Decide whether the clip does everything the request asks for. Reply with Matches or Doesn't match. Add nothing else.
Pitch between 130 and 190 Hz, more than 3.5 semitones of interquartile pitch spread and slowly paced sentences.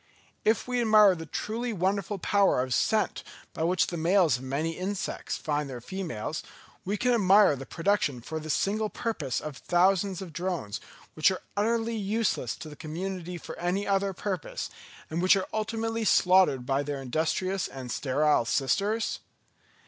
Doesn't match